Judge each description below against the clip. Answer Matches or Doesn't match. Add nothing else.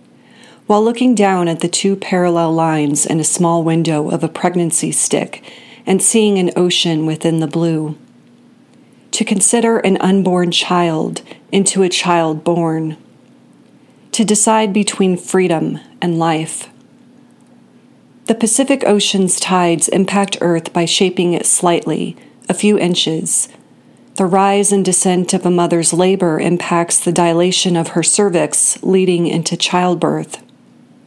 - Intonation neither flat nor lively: Matches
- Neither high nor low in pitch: Matches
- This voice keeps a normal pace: Doesn't match